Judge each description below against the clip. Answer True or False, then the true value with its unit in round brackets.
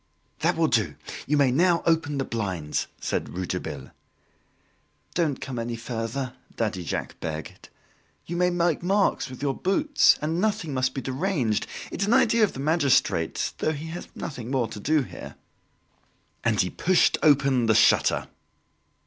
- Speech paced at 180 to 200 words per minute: False (155 wpm)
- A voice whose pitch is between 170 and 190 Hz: False (140 Hz)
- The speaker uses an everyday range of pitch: False (6.6 semitones)